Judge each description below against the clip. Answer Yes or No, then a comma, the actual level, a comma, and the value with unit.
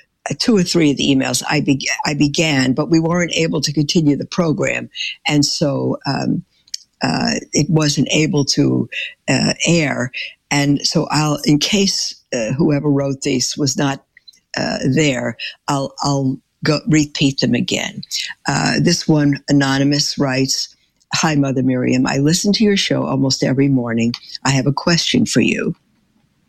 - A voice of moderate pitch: Yes, medium, 145 Hz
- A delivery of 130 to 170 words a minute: Yes, average, 160 wpm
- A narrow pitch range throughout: Yes, narrow, 2.3 semitones